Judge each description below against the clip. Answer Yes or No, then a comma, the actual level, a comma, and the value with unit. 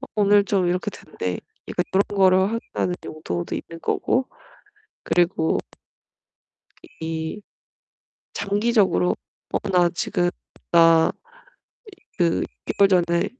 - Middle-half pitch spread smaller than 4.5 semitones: Yes, average, 3.2 semitones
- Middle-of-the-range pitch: Yes, medium, 180 Hz